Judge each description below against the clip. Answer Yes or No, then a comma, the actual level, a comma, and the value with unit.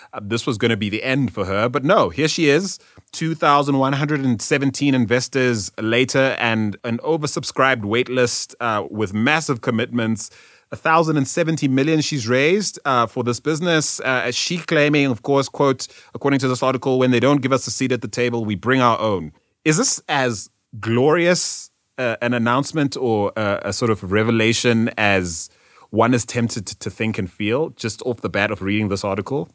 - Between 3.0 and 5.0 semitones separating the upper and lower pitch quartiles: Yes, average, 4.0 semitones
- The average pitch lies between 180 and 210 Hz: No, low, 125 Hz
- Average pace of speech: Yes, average, 175 wpm